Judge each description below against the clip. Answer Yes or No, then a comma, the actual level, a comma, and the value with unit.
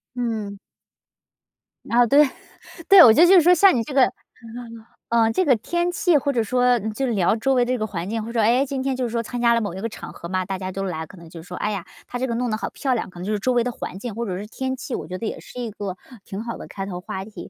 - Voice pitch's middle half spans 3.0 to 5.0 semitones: Yes, average, 4.2 semitones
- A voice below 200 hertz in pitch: No, high, 230 Hz